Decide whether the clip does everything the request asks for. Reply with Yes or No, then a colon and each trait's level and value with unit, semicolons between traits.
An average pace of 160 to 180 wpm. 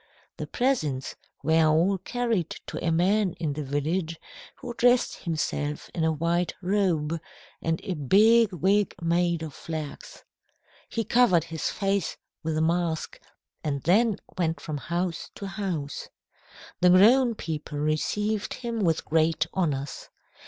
No: average, 140 wpm